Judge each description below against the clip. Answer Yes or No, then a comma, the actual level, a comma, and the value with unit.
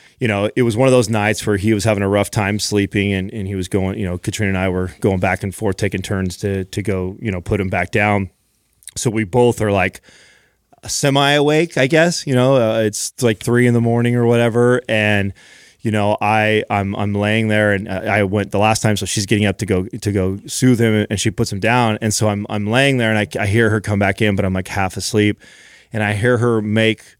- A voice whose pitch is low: Yes, low, 105 Hz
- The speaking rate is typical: No, fast, 255 wpm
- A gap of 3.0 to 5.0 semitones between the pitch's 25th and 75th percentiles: No, narrow, 2.5 semitones